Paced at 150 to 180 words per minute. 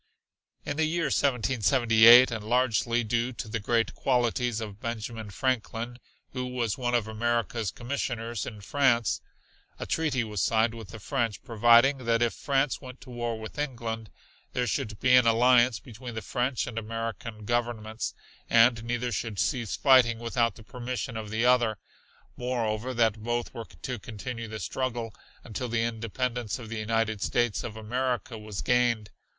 Yes: average, 160 wpm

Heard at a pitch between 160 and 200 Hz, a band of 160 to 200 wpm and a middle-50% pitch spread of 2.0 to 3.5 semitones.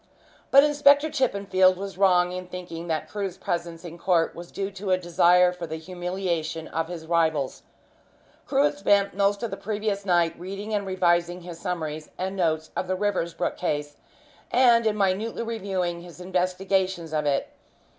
Yes: medium, 185 Hz; average, 165 wpm; average, 2.7 semitones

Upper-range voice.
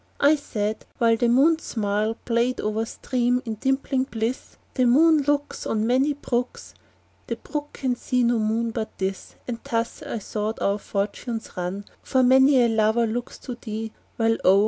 Yes: high, 235 Hz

